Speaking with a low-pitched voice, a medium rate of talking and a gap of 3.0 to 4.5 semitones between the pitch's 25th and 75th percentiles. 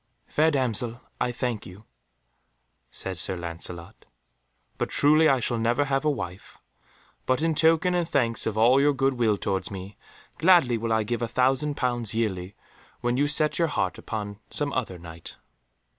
No: low, 120 Hz; average, 170 wpm; wide, 5.6 semitones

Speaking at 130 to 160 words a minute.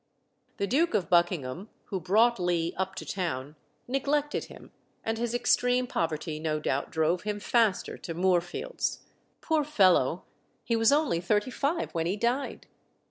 Yes: average, 150 wpm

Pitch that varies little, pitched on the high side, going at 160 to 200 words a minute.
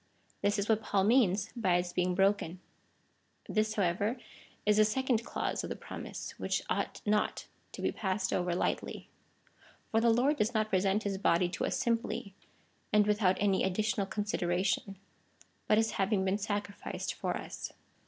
Yes: narrow, 2.3 semitones; high, 205 Hz; average, 170 wpm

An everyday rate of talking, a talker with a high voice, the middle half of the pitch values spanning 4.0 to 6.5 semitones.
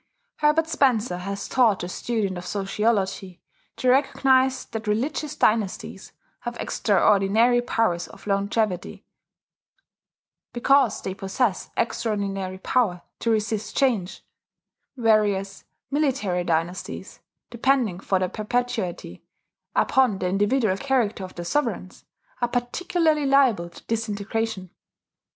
No: slow, 105 wpm; high, 215 Hz; average, 4.5 semitones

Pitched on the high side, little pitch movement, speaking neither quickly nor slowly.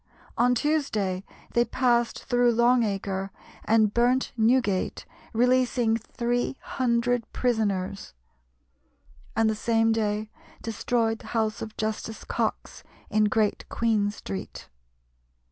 No: high, 225 Hz; narrow, 2.3 semitones; slow, 110 wpm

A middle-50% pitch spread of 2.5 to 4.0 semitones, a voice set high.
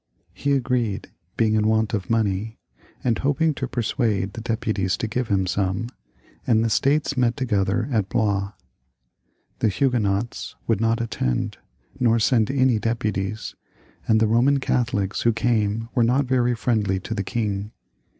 No: average, 2.9 semitones; low, 115 Hz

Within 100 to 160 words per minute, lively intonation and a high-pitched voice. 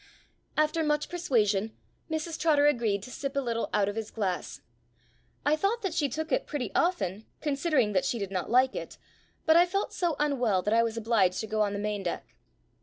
No: fast, 205 wpm; wide, 6.7 semitones; very high, 250 Hz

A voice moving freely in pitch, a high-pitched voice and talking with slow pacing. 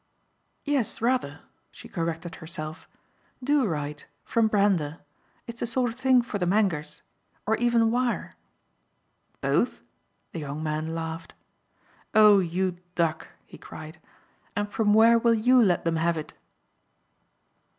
Yes: wide, 6.1 semitones; high, 195 Hz; slow, 130 wpm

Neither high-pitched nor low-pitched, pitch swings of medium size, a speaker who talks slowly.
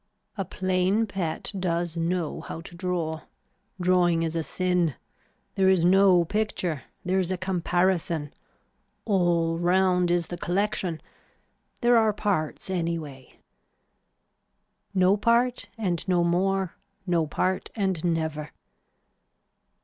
No: medium, 180 Hz; narrow, 2.3 semitones; slow, 115 wpm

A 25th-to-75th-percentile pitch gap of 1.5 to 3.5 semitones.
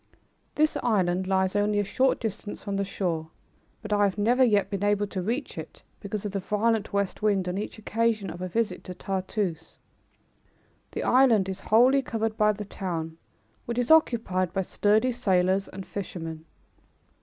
Yes: average, 2.9 semitones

